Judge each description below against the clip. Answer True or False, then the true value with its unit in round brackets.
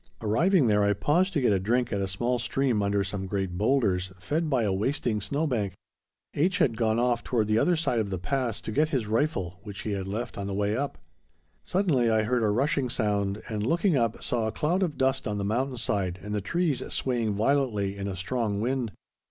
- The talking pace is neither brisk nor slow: False (225 wpm)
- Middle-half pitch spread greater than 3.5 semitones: True (4.9 semitones)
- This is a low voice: True (115 Hz)